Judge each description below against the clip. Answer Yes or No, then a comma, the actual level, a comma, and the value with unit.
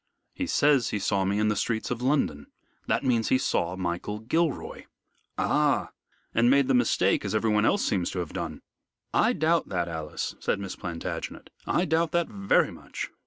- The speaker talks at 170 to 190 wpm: Yes, average, 180 wpm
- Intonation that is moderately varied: No, wide, 6.4 semitones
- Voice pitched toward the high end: No, low, 110 Hz